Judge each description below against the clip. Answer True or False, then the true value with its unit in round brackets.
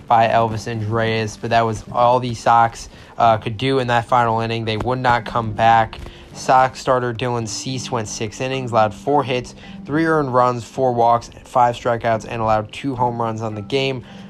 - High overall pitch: False (120 Hz)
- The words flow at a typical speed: True (195 wpm)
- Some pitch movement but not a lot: False (2.2 semitones)